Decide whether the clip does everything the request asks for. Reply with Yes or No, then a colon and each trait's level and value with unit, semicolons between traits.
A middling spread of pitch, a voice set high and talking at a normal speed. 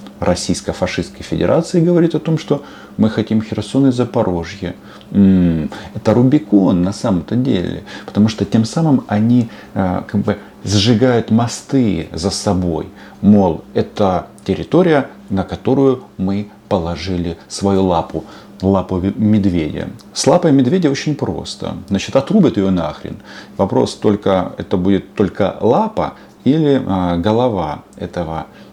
No: average, 4.1 semitones; low, 100 Hz; average, 120 wpm